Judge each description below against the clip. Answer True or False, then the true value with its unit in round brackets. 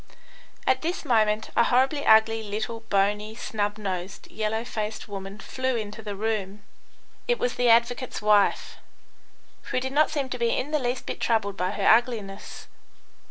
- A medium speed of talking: True (160 wpm)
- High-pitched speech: True (220 Hz)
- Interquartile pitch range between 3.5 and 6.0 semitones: False (3.0 semitones)